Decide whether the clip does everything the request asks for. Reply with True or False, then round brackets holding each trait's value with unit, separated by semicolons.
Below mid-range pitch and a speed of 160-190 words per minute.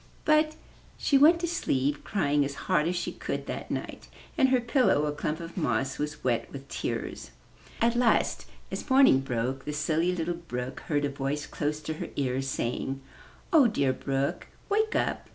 False (150 Hz; 180 wpm)